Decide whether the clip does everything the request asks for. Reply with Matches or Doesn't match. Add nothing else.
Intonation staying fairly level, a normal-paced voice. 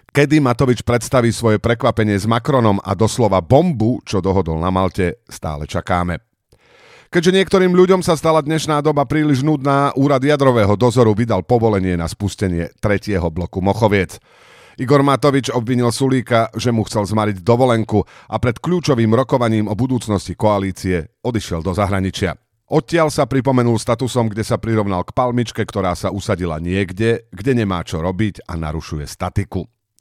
Doesn't match